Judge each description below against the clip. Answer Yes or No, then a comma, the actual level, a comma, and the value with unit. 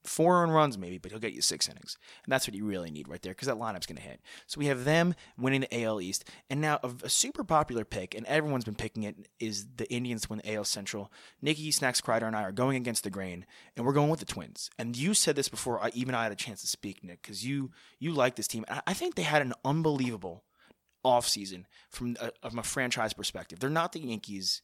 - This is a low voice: Yes, low, 120 Hz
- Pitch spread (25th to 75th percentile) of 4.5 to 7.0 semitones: Yes, average, 4.9 semitones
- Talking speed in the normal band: No, fast, 255 wpm